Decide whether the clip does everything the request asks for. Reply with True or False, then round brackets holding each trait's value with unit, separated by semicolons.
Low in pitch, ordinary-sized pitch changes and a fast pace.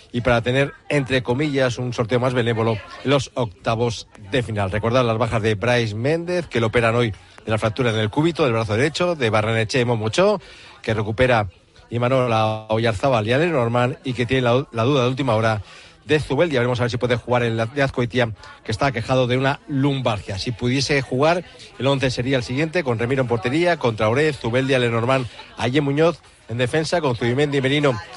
True (125 Hz; 3.4 semitones; 200 wpm)